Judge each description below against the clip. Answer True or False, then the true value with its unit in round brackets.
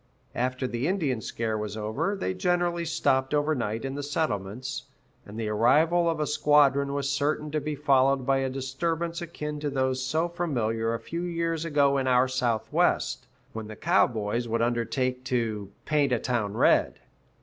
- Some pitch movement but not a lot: True (4.6 semitones)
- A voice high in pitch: False (135 Hz)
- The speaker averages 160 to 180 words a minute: True (170 wpm)